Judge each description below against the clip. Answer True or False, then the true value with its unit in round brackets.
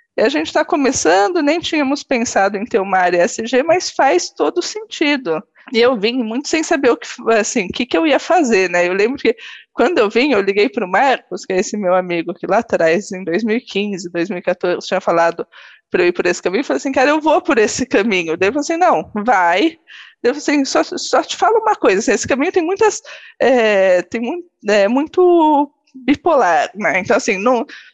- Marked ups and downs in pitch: True (8.5 semitones)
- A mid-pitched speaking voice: False (255 Hz)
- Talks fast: True (210 wpm)